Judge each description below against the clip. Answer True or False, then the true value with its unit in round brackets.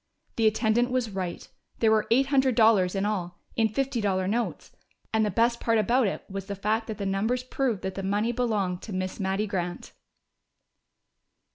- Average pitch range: True (3.2 semitones)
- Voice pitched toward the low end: False (215 Hz)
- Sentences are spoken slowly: False (185 wpm)